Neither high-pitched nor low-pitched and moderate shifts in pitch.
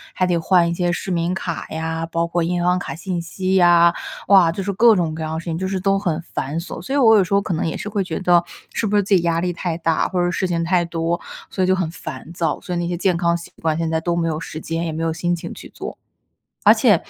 No: medium, 175 Hz; narrow, 2.0 semitones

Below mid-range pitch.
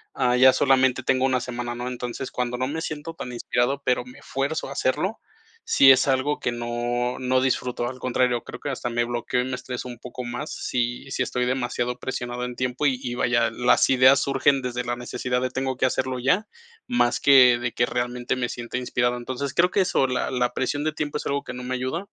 Yes: low, 125 Hz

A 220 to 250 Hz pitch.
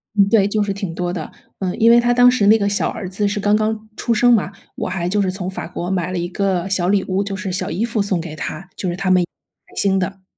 No: high, 195 Hz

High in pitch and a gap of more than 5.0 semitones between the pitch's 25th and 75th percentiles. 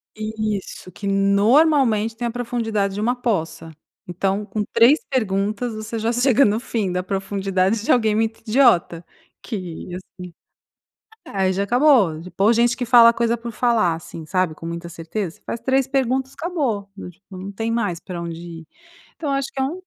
No: high, 215 Hz; average, 4.3 semitones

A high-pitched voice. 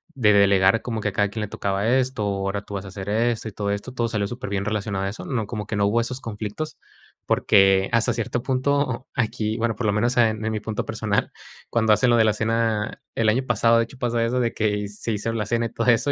No: low, 110 Hz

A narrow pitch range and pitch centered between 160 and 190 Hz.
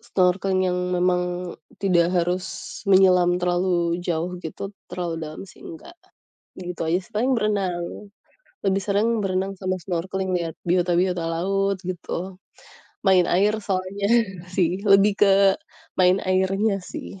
Yes: narrow, 1.8 semitones; medium, 185 Hz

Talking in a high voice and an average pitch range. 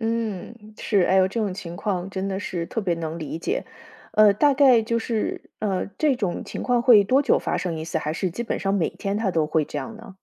Yes: high, 195 Hz; average, 4.7 semitones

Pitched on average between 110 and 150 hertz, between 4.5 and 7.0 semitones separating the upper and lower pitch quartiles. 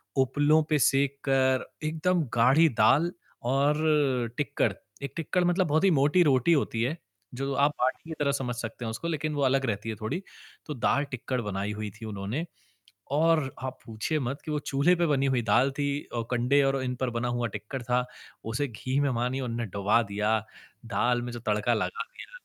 No: low, 135 Hz; average, 3.9 semitones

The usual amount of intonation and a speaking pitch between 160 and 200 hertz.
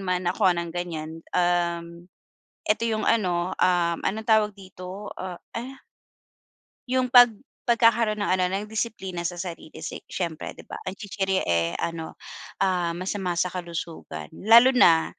Yes: average, 3.7 semitones; medium, 185 Hz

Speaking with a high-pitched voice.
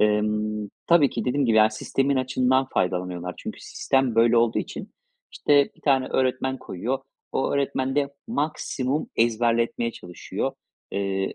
No: low, 120 Hz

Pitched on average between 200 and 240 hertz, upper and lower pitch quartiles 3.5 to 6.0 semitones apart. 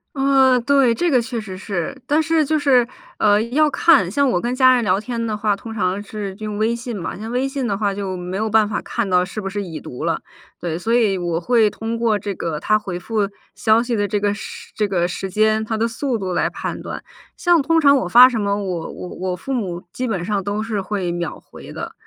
Yes: high, 215 Hz; average, 4.1 semitones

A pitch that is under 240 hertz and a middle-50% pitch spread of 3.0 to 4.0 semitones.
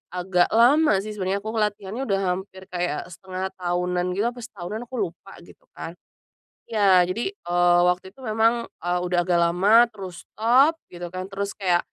Yes: high, 190 Hz; average, 3.7 semitones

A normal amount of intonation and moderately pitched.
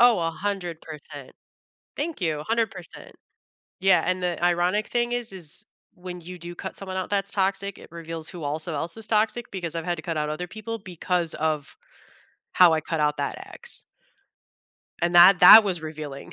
Yes: average, 3.6 semitones; medium, 175 Hz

